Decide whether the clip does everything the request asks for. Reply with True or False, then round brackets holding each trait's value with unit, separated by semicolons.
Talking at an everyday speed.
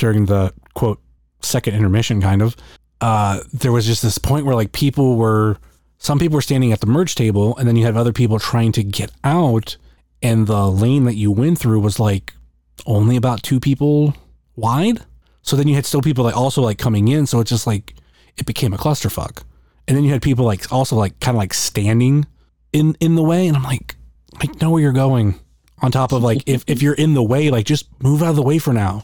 False (230 wpm)